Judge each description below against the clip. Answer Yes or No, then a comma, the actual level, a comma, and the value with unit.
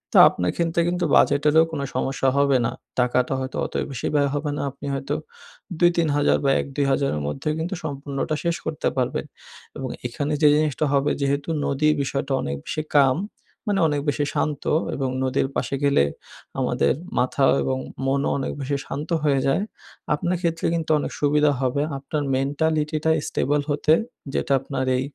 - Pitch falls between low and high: Yes, medium, 145 Hz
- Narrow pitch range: Yes, narrow, 2.1 semitones